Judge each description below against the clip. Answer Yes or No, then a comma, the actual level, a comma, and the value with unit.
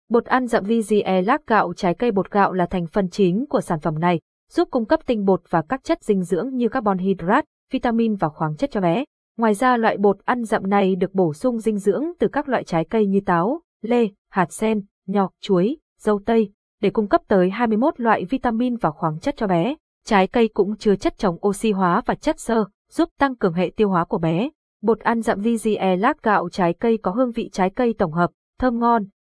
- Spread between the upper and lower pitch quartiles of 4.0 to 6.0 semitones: Yes, average, 4.4 semitones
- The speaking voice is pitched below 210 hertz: No, high, 215 Hz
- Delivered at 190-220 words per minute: No, average, 230 wpm